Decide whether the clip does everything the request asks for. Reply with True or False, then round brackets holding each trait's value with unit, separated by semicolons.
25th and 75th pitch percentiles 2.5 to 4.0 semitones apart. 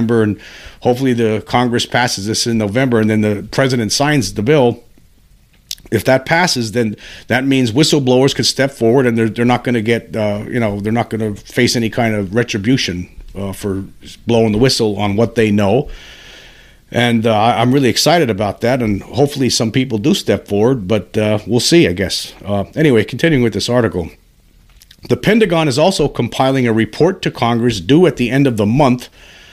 True (3.5 semitones)